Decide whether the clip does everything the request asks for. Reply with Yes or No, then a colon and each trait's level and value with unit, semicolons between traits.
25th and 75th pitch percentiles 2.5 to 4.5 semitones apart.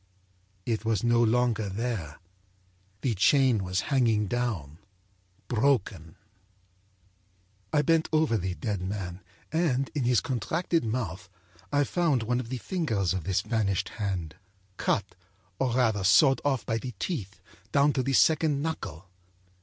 No: wide, 5.6 semitones